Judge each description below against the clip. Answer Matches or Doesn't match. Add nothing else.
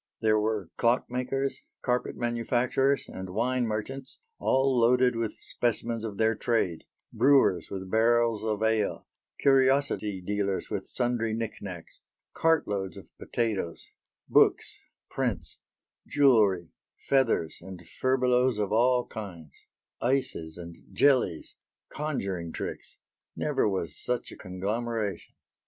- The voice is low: Matches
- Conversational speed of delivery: Doesn't match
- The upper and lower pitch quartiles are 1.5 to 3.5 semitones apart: Doesn't match